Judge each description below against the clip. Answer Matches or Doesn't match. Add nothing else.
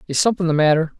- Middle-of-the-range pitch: Matches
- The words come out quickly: Matches